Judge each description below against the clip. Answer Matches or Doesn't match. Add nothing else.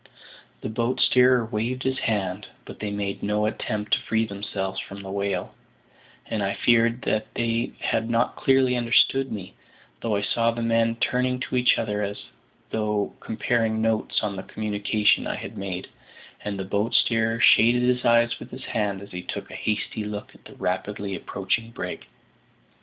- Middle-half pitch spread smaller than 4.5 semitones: Matches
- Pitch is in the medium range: Doesn't match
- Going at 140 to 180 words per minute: Matches